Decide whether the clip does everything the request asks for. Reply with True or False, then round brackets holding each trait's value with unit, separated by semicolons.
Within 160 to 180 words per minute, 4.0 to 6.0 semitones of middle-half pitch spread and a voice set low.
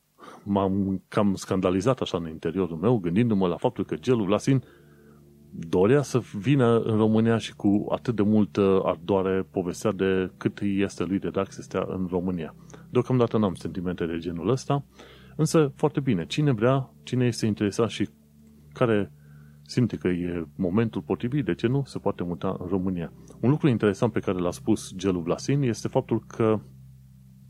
True (165 wpm; 5.3 semitones; 100 Hz)